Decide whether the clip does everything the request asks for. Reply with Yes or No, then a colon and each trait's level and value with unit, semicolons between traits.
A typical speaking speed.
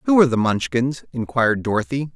Yes: average, 165 wpm